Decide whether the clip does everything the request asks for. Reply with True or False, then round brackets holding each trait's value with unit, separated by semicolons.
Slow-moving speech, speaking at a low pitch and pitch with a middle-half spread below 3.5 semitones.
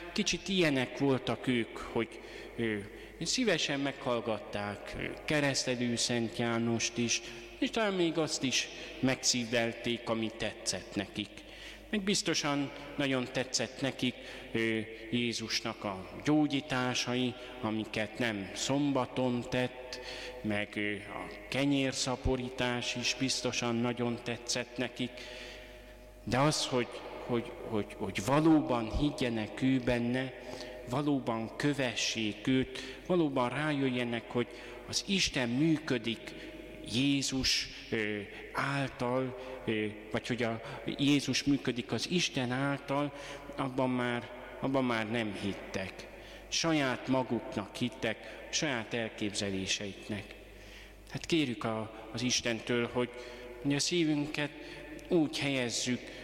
True (100 wpm; 125 Hz; 2.9 semitones)